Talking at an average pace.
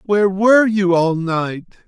Yes: average, 160 wpm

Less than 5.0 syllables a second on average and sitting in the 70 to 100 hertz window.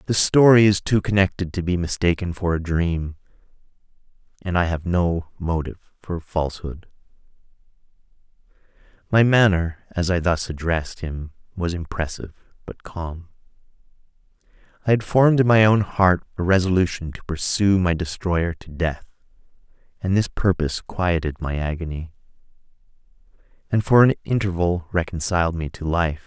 No: 5.1 syllables/s; very low, 90 Hz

